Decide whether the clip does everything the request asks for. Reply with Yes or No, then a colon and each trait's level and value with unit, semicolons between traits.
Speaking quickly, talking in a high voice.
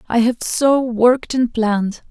No: average, 170 wpm; high, 235 Hz